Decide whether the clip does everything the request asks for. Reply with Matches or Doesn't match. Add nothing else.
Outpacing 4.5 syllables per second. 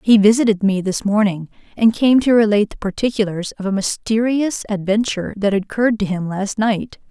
Matches